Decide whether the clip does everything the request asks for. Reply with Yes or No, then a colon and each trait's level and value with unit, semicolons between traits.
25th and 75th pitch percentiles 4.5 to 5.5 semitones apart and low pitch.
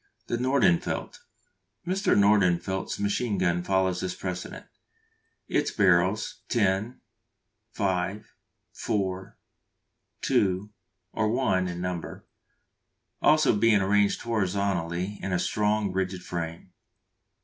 No: narrow, 2.5 semitones; very low, 95 Hz